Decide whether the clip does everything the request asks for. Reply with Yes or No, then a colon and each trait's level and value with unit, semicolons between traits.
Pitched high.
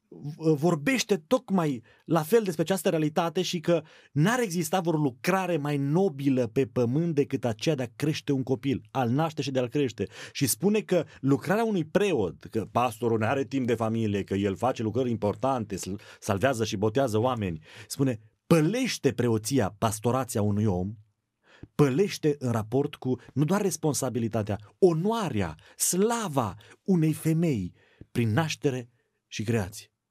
No: low, 135 Hz